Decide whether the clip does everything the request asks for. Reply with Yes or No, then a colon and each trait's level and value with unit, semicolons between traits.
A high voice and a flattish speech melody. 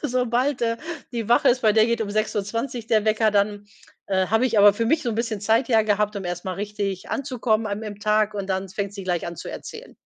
Yes: high, 215 Hz; narrow, 2.3 semitones